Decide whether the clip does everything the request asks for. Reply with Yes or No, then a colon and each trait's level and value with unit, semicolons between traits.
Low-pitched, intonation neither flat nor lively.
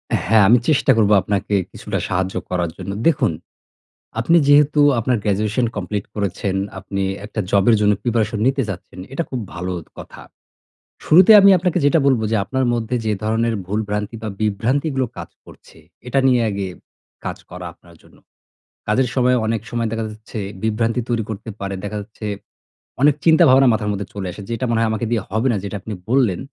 Yes: low, 110 Hz; average, 3.8 semitones